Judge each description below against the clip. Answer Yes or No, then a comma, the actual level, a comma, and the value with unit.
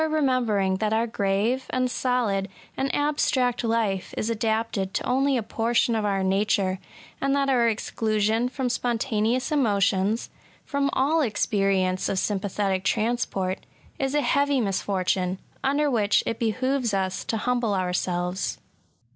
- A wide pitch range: No, average, 4.5 semitones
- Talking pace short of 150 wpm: Yes, average, 140 wpm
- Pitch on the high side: Yes, high, 225 Hz